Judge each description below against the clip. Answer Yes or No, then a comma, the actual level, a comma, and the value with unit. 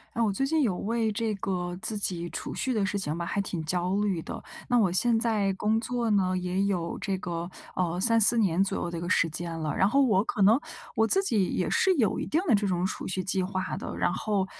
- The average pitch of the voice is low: No, high, 195 Hz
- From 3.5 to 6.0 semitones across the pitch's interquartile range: Yes, average, 3.8 semitones